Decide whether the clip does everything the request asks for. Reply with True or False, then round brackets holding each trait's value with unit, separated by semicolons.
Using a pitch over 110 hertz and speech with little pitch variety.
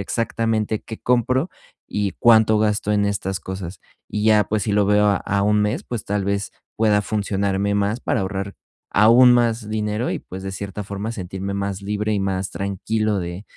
False (105 Hz; 1.7 semitones)